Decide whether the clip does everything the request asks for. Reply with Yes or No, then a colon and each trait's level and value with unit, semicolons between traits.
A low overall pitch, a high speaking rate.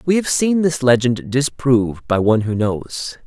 No: low, 130 Hz; average, 185 wpm